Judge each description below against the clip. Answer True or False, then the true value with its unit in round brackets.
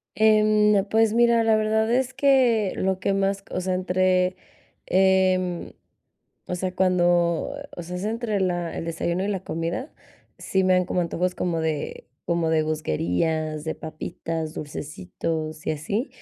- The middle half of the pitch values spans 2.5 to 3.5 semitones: False (4.2 semitones)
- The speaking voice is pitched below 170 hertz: False (185 Hz)